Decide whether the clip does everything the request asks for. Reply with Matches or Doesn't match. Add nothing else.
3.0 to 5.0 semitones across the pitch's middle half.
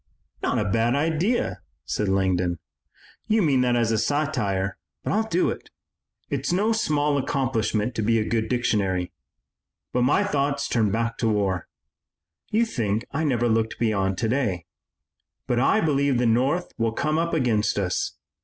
Doesn't match